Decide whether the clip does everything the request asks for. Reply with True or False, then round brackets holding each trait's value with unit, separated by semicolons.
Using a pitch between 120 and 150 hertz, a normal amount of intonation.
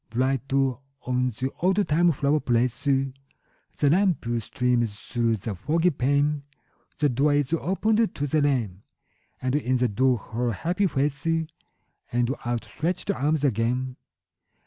True (135 Hz; 3.5 semitones)